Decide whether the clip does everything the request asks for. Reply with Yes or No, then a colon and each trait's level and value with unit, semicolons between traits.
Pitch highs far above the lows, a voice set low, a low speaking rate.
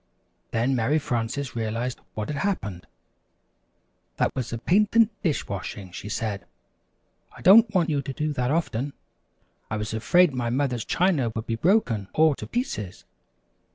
No: wide, 6.1 semitones; low, 130 Hz; average, 155 wpm